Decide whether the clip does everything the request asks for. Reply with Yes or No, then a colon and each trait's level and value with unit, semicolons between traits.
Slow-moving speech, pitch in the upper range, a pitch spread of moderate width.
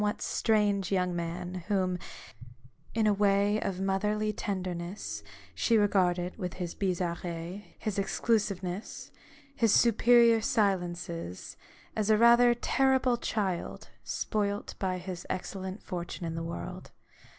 Yes: slow, 120 wpm; high, 195 Hz; average, 3.1 semitones